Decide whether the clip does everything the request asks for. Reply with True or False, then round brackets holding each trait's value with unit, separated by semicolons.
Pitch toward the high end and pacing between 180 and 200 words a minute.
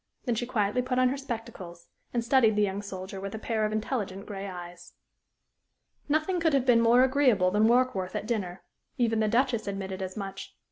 True (220 Hz; 195 wpm)